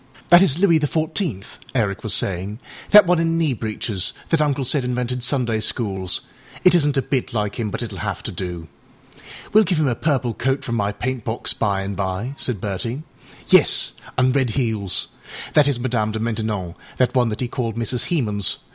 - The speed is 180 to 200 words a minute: Yes, average, 190 wpm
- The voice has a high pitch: No, low, 120 Hz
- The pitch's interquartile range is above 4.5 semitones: Yes, average, 5.1 semitones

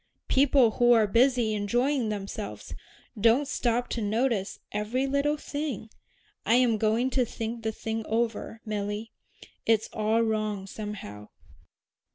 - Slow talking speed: Yes, slow, 130 wpm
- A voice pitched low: No, high, 225 Hz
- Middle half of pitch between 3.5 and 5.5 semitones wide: No, average, 2.7 semitones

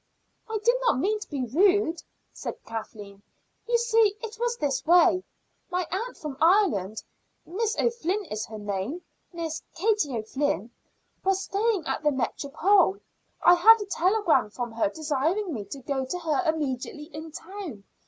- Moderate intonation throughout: No, wide, 7.5 semitones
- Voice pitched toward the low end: No, very high, 330 Hz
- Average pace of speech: Yes, average, 155 wpm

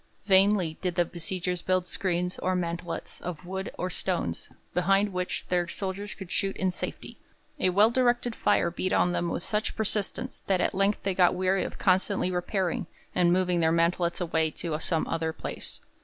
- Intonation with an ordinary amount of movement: No, narrow, 2.0 semitones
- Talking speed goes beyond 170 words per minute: Yes, average, 180 wpm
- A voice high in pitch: No, medium, 180 Hz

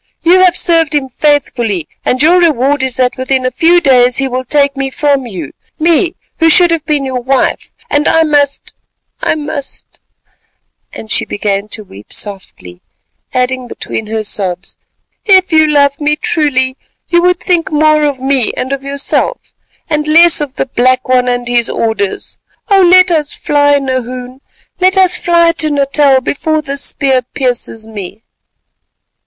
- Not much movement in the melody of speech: No, average, 3.8 semitones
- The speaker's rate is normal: Yes, average, 160 wpm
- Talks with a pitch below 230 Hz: No, very high, 275 Hz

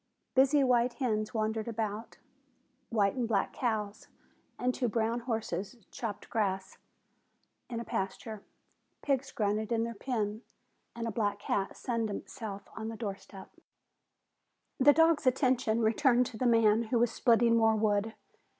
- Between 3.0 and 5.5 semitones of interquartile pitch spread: No, narrow, 2.4 semitones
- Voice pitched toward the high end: Yes, high, 225 Hz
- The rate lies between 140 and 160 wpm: Yes, average, 145 wpm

